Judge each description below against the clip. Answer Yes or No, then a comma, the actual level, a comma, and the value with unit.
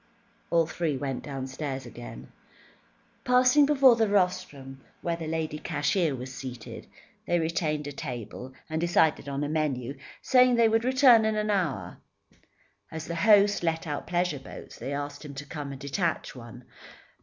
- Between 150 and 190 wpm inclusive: Yes, average, 160 wpm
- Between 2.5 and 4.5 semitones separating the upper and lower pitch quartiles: No, wide, 5.6 semitones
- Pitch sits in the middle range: Yes, medium, 155 Hz